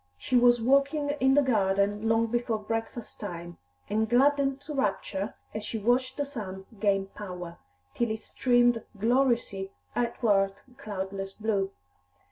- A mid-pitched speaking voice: No, high, 225 Hz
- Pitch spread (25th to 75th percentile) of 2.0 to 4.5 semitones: Yes, average, 4.1 semitones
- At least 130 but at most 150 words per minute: Yes, slow, 135 wpm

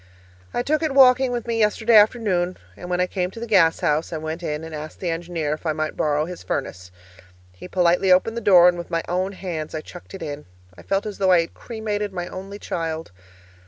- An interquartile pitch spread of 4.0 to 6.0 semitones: Yes, average, 4.3 semitones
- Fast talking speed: Yes, fast, 235 wpm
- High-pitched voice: No, medium, 180 Hz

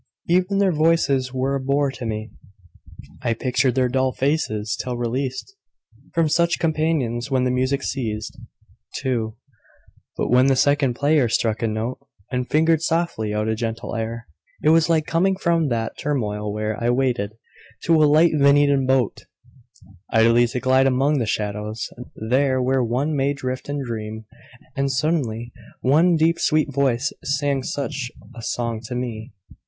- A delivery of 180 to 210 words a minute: No, average, 160 wpm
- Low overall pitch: Yes, low, 130 Hz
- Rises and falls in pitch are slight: No, average, 3.9 semitones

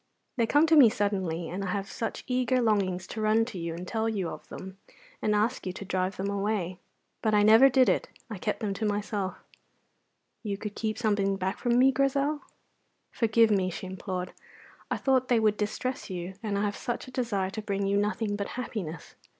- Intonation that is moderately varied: Yes, average, 3.1 semitones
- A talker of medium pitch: No, high, 210 Hz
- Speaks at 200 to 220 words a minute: Yes, fast, 205 wpm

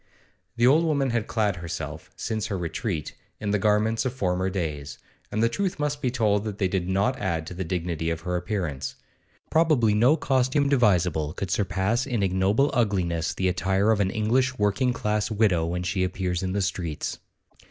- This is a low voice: Yes, low, 100 Hz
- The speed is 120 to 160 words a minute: No, average, 185 wpm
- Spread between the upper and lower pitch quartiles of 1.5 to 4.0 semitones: No, average, 4.6 semitones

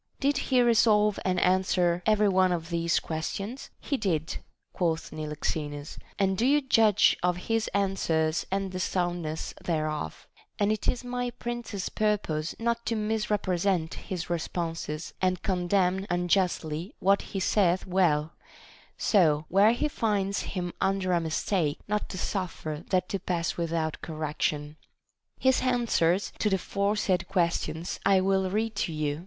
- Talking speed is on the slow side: No, average, 150 wpm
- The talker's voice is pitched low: No, medium, 185 Hz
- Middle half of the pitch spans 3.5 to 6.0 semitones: Yes, average, 3.9 semitones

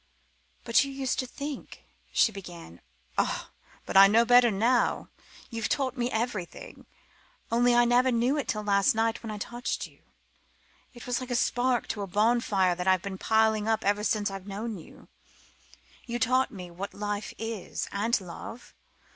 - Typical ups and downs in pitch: Yes, average, 3.4 semitones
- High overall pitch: Yes, high, 225 Hz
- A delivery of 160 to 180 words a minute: Yes, average, 175 wpm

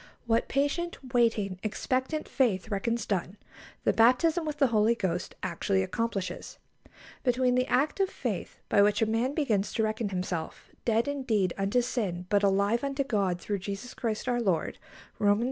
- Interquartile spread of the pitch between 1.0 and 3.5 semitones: No, average, 4.4 semitones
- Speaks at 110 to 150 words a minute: No, average, 165 wpm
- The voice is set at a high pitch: Yes, high, 225 Hz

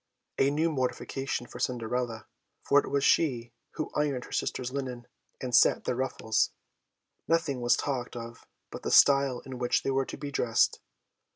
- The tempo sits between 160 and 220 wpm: Yes, average, 170 wpm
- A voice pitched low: Yes, low, 130 Hz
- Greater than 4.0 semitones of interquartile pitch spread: No, narrow, 2.5 semitones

